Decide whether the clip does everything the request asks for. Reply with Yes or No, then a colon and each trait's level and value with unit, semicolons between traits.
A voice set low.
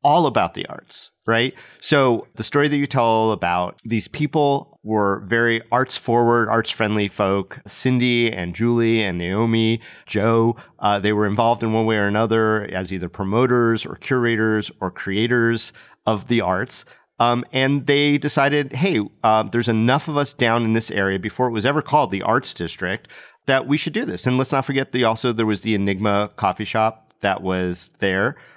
Yes: low, 115 Hz